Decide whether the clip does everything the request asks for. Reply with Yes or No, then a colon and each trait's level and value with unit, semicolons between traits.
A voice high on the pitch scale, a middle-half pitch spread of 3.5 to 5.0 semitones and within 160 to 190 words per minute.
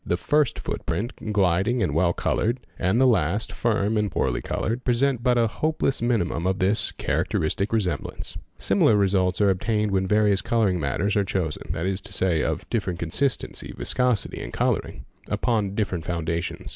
No: low, 100 Hz; average, 4.2 semitones; average, 170 wpm